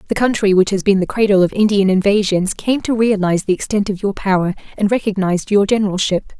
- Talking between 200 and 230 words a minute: Yes, fast, 205 wpm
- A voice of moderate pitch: No, high, 200 Hz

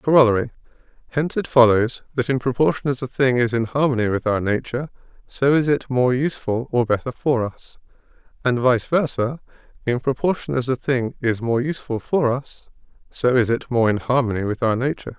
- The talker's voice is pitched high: No, low, 125 Hz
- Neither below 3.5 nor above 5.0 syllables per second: No, 5.6 syllables/s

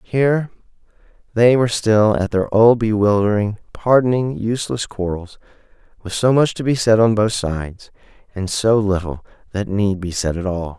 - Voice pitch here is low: Yes, low, 105 Hz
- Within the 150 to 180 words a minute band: Yes, average, 160 wpm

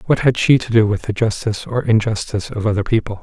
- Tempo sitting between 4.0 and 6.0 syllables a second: No, 6.5 syllables/s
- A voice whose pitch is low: Yes, low, 110 Hz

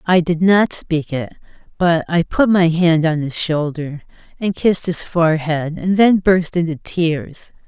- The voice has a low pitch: No, medium, 170 Hz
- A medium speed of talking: Yes, average, 170 wpm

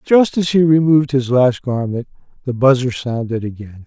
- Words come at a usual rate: Yes, average, 170 wpm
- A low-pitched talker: Yes, low, 130 Hz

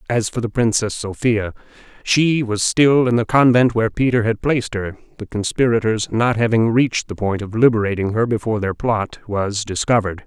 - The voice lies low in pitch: Yes, low, 110 Hz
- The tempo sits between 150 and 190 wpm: Yes, average, 180 wpm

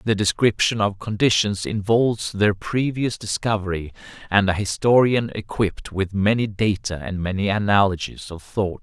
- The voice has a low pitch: Yes, low, 105 Hz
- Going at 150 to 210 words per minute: No, slow, 135 wpm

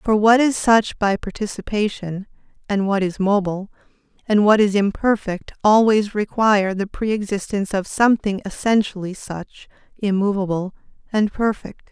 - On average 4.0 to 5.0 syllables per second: Yes, 4.9 syllables/s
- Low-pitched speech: No, high, 205 Hz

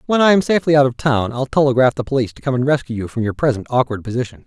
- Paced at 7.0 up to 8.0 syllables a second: Yes, 7.5 syllables/s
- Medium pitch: No, low, 130 Hz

